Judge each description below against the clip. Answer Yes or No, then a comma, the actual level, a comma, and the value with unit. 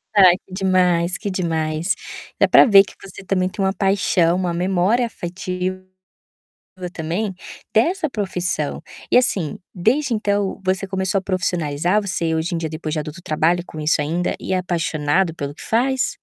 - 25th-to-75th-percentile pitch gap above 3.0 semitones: No, average, 2.7 semitones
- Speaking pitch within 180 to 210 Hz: Yes, medium, 185 Hz